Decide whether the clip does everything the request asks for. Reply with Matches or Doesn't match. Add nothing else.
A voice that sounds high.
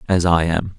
Doesn't match